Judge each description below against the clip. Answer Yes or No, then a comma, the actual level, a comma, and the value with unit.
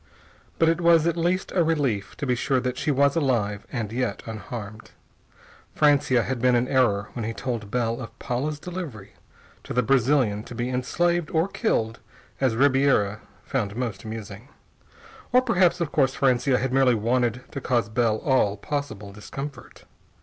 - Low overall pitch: Yes, low, 125 Hz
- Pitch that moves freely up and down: No, average, 4.3 semitones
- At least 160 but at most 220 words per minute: Yes, average, 165 wpm